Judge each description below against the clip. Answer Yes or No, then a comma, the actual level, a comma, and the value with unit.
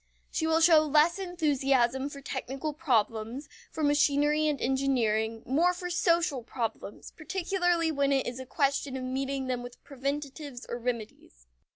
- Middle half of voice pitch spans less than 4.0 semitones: Yes, average, 3.5 semitones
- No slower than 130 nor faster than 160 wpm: Yes, average, 150 wpm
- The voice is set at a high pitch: Yes, very high, 275 Hz